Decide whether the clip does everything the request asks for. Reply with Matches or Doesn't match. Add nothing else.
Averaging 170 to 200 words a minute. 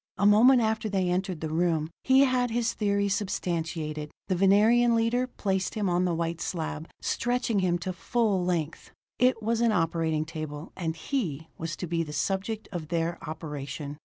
Matches